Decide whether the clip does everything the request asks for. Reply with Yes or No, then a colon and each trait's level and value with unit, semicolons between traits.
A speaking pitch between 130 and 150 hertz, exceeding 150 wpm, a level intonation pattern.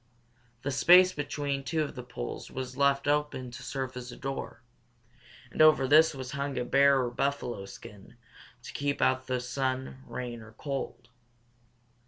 Yes: low, 135 Hz; average, 165 wpm; narrow, 2.1 semitones